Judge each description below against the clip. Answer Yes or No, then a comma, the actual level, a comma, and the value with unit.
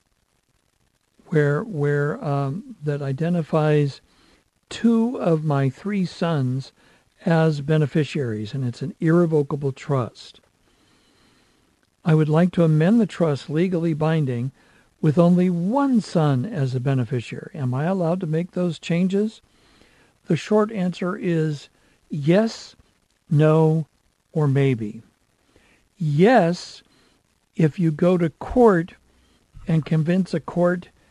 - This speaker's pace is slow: Yes, slow, 110 wpm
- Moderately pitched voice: Yes, medium, 160 Hz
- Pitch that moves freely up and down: No, average, 3.6 semitones